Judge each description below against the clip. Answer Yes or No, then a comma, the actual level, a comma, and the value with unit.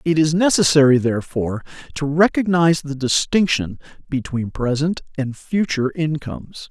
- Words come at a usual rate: No, slow, 115 wpm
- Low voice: No, medium, 150 Hz